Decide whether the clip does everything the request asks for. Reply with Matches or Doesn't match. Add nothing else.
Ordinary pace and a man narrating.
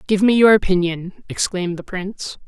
Doesn't match